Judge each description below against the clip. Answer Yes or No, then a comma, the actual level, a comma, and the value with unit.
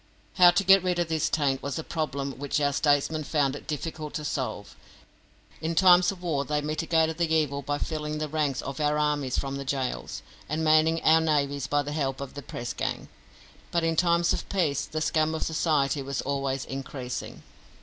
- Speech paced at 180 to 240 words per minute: Yes, average, 200 wpm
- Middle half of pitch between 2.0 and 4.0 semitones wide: Yes, narrow, 2.5 semitones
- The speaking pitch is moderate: Yes, medium, 150 Hz